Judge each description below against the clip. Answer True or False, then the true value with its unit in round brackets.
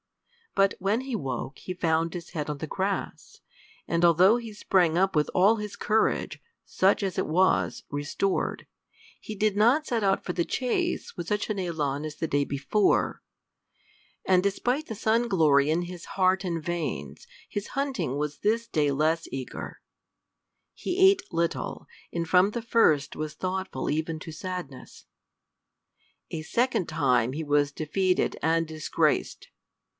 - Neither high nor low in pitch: True (180 Hz)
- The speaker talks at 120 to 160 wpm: True (155 wpm)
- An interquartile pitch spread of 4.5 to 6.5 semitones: True (5.1 semitones)